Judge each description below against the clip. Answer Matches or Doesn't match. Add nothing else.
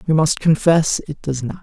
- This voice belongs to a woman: Doesn't match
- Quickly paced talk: Matches